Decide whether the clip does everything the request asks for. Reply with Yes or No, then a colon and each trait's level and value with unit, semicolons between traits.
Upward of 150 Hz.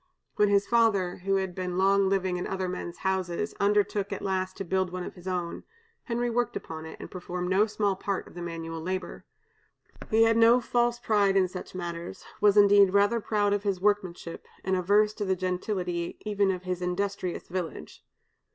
Yes: high, 190 Hz